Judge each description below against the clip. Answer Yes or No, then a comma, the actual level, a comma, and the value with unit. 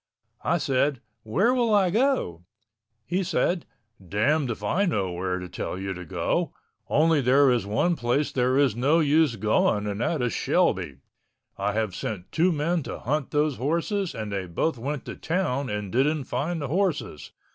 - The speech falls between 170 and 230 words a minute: Yes, average, 180 wpm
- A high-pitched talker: No, low, 135 Hz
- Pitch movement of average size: No, wide, 7.7 semitones